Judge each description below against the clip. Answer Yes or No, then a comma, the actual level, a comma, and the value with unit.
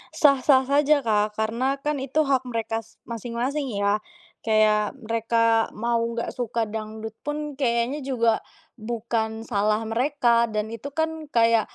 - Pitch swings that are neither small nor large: Yes, average, 3.3 semitones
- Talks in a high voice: Yes, high, 235 Hz